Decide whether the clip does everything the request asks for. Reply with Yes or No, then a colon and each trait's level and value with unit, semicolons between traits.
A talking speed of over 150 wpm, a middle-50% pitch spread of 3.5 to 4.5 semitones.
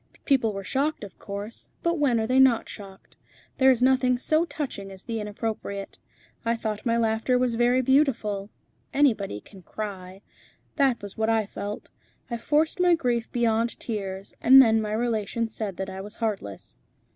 Yes: average, 170 wpm; average, 3.8 semitones